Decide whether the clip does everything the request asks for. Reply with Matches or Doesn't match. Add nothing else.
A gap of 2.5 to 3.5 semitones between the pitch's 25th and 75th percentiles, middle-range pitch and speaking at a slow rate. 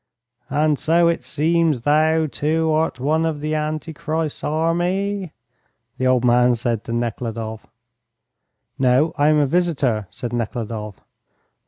Doesn't match